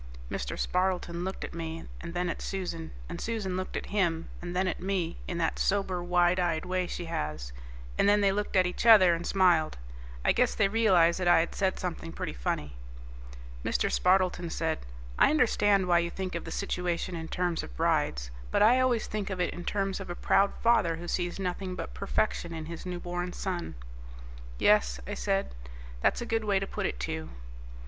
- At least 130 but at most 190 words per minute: No, average, 200 wpm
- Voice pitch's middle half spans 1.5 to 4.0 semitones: Yes, narrow, 2.5 semitones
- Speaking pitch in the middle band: Yes, medium, 180 Hz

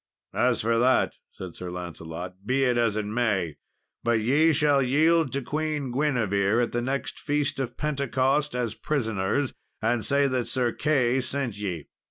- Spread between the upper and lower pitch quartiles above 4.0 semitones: Yes, average, 4.7 semitones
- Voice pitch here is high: No, low, 125 Hz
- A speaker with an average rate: Yes, average, 165 wpm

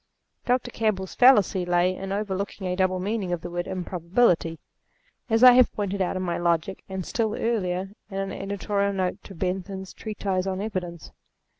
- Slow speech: No, average, 170 wpm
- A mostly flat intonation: Yes, narrow, 2.2 semitones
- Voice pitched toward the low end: No, high, 190 Hz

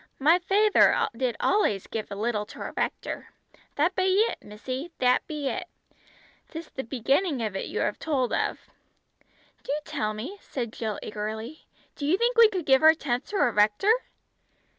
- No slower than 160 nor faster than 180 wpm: Yes, average, 175 wpm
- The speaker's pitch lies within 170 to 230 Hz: No, very high, 270 Hz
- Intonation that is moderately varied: No, wide, 8.1 semitones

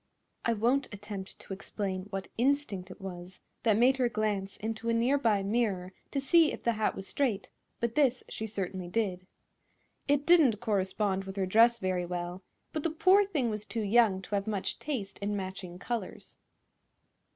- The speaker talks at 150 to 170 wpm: No, average, 180 wpm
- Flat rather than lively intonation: No, average, 3.9 semitones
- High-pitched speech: Yes, high, 210 Hz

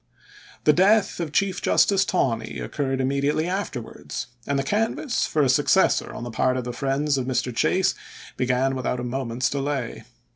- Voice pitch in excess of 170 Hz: No, low, 135 Hz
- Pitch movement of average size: Yes, average, 4.0 semitones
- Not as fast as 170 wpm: No, average, 180 wpm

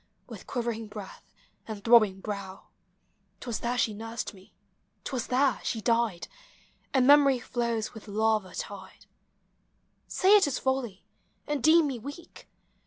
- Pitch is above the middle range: Yes, high, 230 Hz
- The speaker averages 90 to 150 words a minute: Yes, average, 145 wpm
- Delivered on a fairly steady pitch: No, average, 3.9 semitones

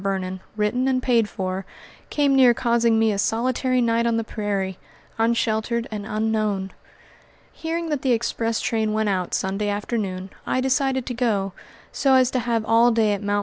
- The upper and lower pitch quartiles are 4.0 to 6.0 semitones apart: No, average, 3.2 semitones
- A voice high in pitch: Yes, high, 225 Hz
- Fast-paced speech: No, average, 175 wpm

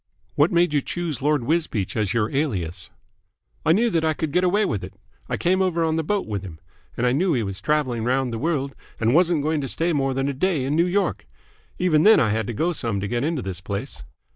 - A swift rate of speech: Yes, fast, 245 wpm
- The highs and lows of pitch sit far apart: Yes, wide, 6.6 semitones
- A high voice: No, medium, 145 Hz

